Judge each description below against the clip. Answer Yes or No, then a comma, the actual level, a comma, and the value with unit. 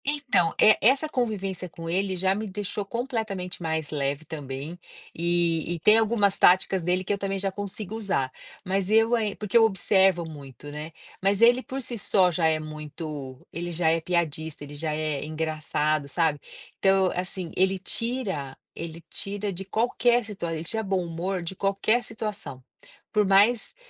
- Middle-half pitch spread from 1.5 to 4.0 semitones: No, average, 4.4 semitones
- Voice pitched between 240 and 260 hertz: No, medium, 185 Hz